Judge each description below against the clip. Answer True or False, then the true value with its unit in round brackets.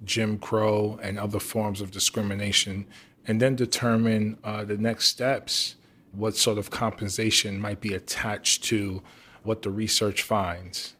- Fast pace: False (140 wpm)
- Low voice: True (105 Hz)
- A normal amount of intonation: False (1.5 semitones)